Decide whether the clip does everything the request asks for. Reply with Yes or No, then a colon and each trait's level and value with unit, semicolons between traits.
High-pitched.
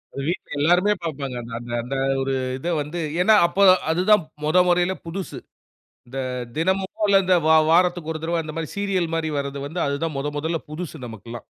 No: medium, 165 Hz